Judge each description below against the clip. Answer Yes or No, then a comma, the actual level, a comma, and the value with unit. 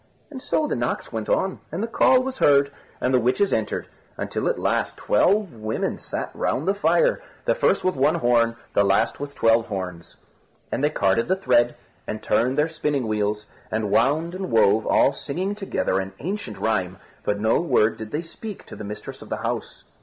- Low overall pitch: Yes, low, 125 Hz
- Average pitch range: No, wide, 8.8 semitones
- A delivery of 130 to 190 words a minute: No, average, 200 wpm